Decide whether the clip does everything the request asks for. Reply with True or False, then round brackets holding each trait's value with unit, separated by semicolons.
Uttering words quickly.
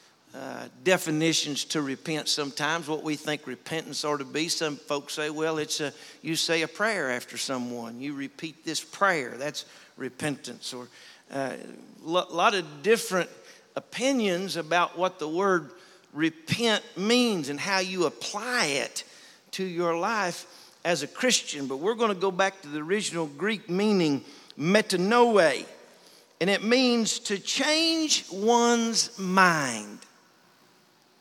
False (140 wpm)